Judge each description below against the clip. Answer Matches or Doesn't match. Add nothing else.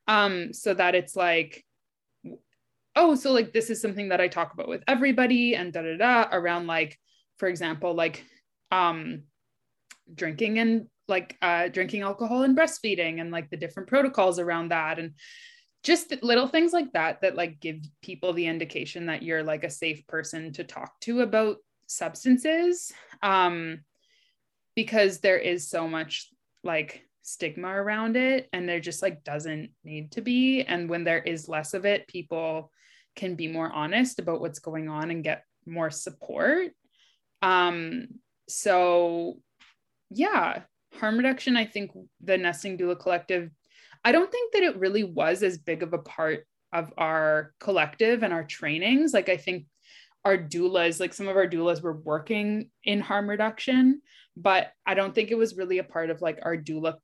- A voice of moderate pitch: Matches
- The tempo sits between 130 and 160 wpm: Doesn't match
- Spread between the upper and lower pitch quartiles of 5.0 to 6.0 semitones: Matches